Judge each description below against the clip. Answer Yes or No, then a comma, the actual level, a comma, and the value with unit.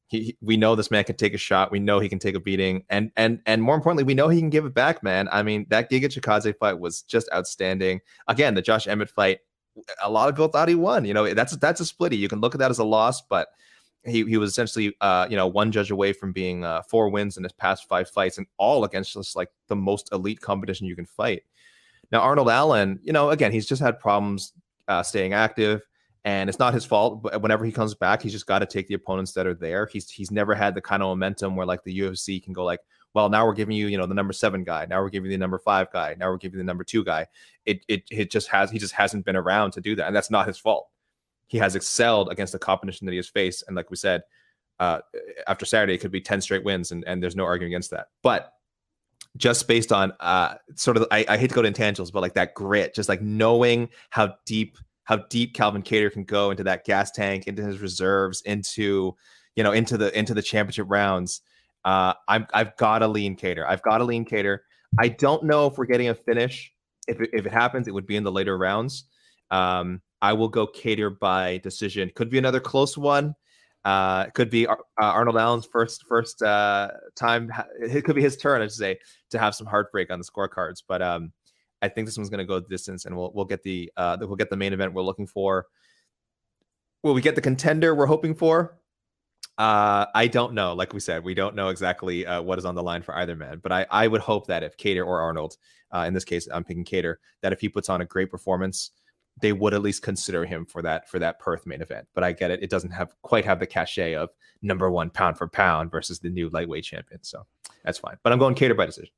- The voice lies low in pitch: Yes, low, 100 Hz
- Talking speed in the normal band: No, fast, 255 wpm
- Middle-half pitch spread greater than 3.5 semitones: No, average, 3.2 semitones